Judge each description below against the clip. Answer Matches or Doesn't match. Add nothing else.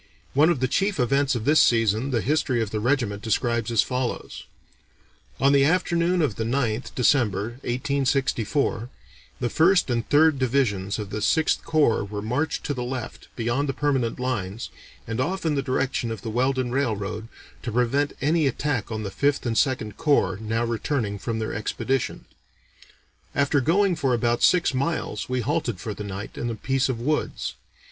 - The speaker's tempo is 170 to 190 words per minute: Matches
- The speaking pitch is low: Matches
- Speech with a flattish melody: Doesn't match